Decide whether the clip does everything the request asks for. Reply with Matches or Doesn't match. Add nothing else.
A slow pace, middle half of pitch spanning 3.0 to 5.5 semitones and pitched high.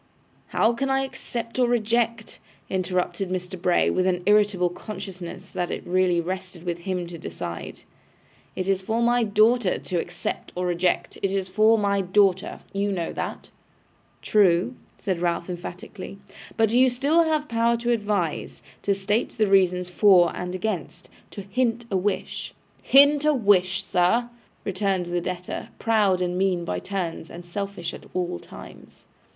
Doesn't match